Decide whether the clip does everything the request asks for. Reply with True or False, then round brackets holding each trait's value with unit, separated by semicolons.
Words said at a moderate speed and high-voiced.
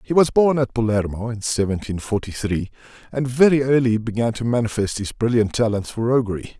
False (180 wpm; 115 Hz)